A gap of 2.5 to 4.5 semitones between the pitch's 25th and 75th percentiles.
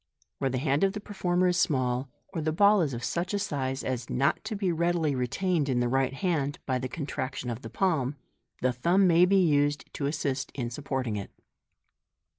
No: average, 5.3 semitones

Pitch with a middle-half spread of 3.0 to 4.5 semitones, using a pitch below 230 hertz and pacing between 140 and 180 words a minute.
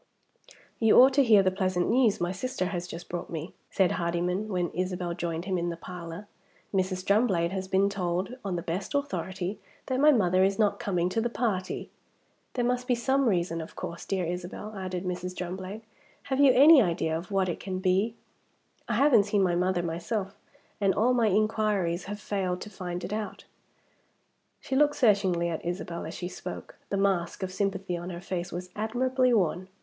No: average, 3.4 semitones; high, 190 Hz; average, 190 wpm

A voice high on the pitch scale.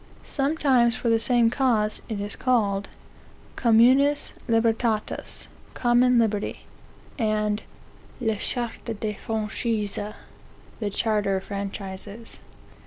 Yes: high, 225 Hz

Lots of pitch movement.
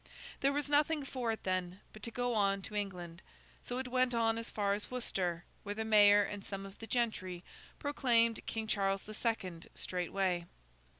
No: average, 3.6 semitones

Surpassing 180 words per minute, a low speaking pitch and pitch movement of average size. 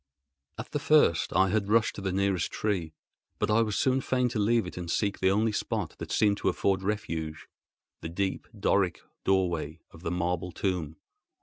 Yes: average, 190 wpm; very low, 95 Hz; average, 3.5 semitones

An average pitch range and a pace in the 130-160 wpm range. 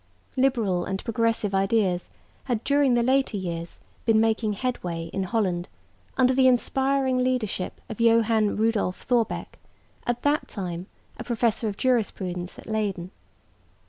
Yes: average, 4.5 semitones; slow, 135 wpm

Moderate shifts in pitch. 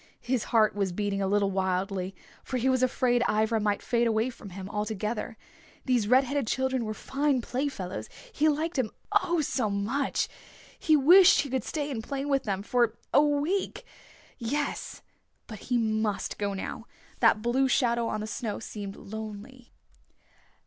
Yes: average, 4.2 semitones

